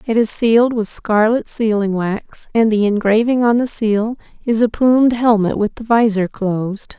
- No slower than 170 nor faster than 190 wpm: Yes, average, 180 wpm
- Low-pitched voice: No, high, 220 Hz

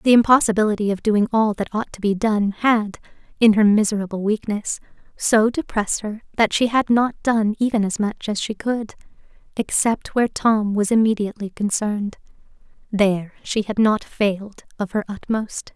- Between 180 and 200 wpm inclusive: No, average, 160 wpm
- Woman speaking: Yes, female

